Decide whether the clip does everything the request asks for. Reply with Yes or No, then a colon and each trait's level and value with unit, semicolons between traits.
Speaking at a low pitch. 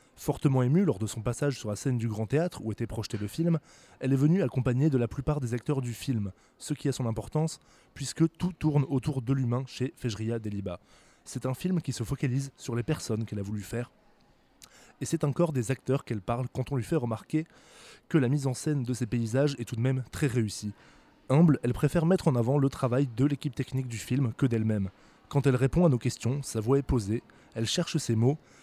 Yes: low, 130 Hz